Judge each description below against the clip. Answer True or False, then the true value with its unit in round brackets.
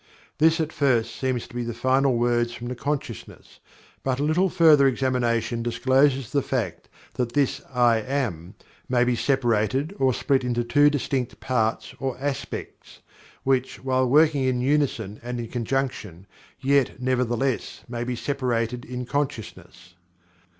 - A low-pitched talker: True (125 Hz)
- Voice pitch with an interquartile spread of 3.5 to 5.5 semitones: False (2.5 semitones)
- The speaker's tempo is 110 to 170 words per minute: True (145 wpm)